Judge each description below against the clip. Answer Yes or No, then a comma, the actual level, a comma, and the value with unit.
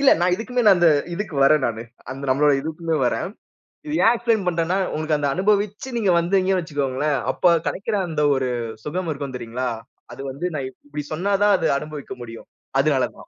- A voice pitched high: No, medium, 160 Hz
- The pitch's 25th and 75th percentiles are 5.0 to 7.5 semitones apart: Yes, wide, 5.6 semitones